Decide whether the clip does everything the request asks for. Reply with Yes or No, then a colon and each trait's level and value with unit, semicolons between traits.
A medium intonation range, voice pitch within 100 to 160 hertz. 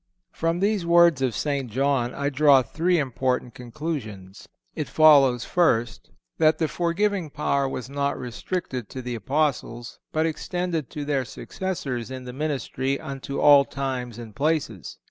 Yes: average, 3.9 semitones; medium, 140 Hz